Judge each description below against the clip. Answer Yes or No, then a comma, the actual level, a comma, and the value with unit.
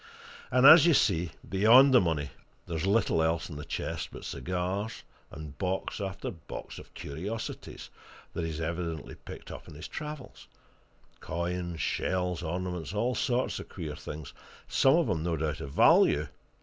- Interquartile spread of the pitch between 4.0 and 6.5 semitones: Yes, average, 4.8 semitones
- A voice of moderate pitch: No, very low, 90 Hz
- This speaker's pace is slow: No, average, 160 wpm